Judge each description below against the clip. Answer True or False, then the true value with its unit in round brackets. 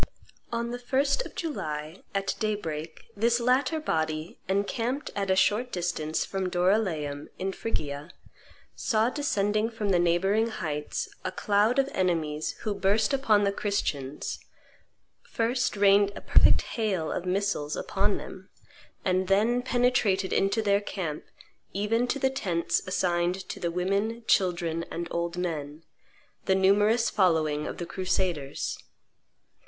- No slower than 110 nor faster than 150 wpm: True (135 wpm)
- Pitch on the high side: True (195 Hz)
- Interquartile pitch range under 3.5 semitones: False (4.7 semitones)